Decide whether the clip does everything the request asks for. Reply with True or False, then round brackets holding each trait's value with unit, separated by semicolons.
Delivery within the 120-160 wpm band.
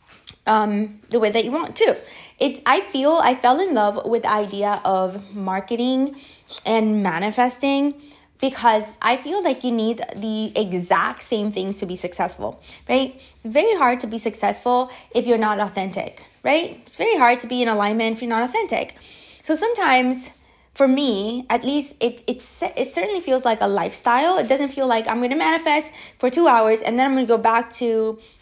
False (190 wpm)